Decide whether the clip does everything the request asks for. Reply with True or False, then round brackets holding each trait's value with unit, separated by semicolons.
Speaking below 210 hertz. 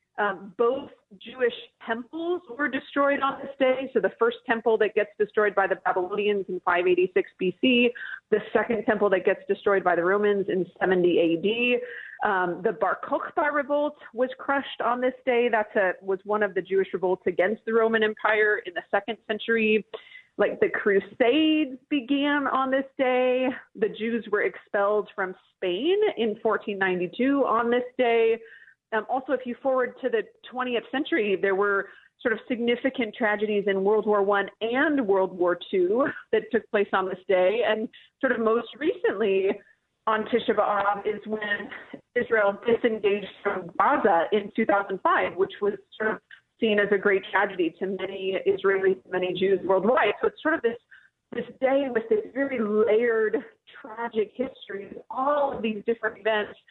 False (220 Hz)